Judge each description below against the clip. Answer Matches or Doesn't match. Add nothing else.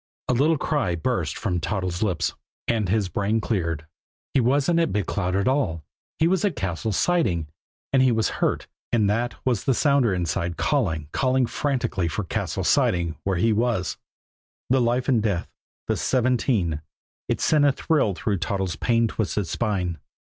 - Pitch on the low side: Matches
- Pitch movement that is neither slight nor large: Doesn't match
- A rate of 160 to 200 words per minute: Matches